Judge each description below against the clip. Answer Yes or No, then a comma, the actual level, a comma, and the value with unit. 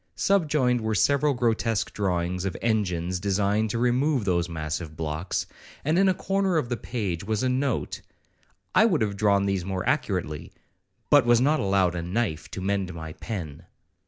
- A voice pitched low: Yes, low, 100 Hz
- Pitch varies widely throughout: Yes, wide, 5.8 semitones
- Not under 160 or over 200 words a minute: Yes, average, 165 wpm